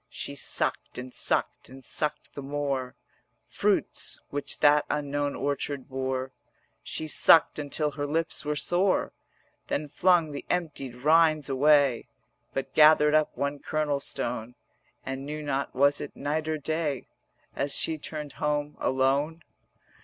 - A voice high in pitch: No, medium, 145 Hz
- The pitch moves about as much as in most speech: No, narrow, 2.1 semitones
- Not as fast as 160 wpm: Yes, average, 140 wpm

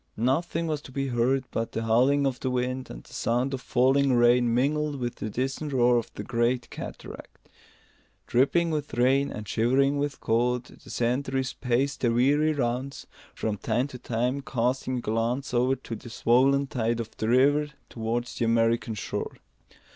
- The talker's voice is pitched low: Yes, low, 125 Hz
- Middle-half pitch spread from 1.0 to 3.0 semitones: Yes, narrow, 2.6 semitones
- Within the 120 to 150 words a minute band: No, average, 170 wpm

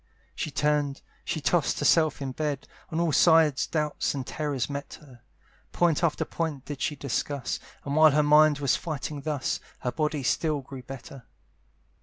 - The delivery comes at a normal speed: Yes, average, 165 wpm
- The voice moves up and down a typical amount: No, narrow, 2.1 semitones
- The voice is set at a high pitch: No, medium, 145 Hz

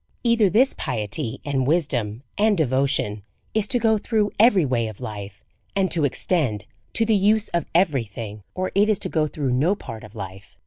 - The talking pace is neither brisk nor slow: Yes, average, 190 wpm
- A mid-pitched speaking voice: Yes, medium, 150 Hz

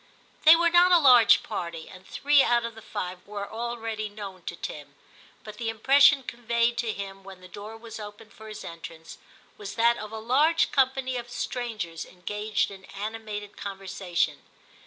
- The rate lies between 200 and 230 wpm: No, average, 175 wpm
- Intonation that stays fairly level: No, average, 3.5 semitones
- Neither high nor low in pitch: No, high, 220 Hz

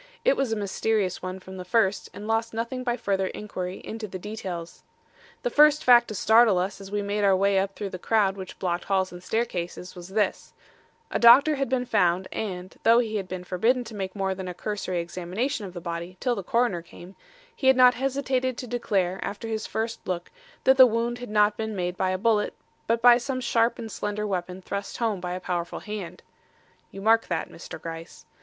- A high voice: Yes, high, 205 Hz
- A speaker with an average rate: No, fast, 215 wpm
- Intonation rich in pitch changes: No, average, 4.0 semitones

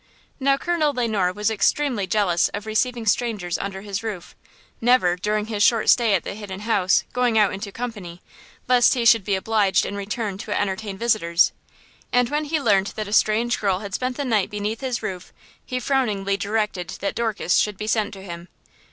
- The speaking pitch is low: No, high, 210 Hz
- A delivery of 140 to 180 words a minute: No, average, 195 wpm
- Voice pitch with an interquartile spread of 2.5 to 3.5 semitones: Yes, average, 3.2 semitones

